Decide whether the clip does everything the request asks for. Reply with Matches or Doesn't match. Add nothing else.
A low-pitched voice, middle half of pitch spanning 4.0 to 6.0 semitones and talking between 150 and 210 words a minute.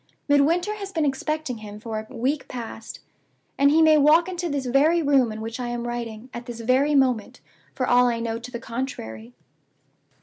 Doesn't match